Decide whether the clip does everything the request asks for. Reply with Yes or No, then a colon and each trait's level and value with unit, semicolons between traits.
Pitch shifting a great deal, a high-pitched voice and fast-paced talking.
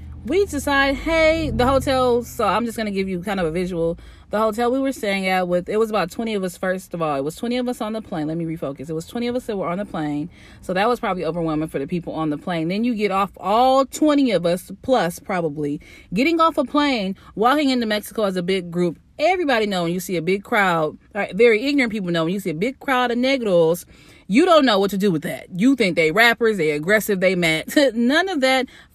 Yes: wide, 6.2 semitones; high, 205 Hz; fast, 260 wpm